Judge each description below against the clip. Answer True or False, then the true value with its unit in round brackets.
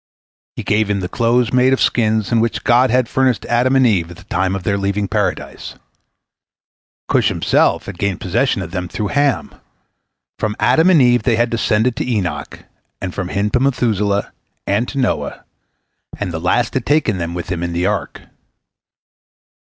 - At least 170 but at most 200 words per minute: True (185 wpm)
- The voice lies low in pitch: True (105 Hz)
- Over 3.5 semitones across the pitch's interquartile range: True (4.6 semitones)